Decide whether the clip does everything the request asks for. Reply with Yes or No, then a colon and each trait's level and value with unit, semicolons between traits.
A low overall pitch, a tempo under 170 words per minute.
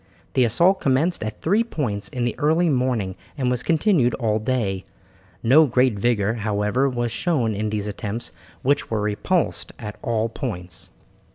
Yes: low, 120 Hz; average, 160 wpm